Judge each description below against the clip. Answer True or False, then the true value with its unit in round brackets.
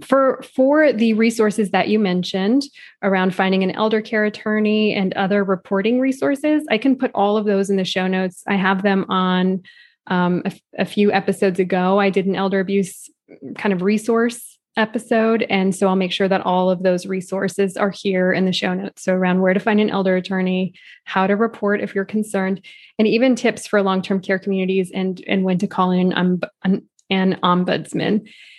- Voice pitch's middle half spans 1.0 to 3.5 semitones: True (2.5 semitones)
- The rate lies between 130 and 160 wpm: False (200 wpm)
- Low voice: False (195 Hz)